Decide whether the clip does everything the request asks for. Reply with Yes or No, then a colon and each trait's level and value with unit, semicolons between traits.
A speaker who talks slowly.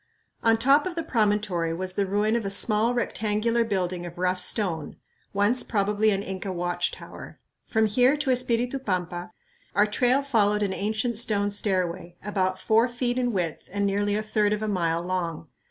No: average, 180 wpm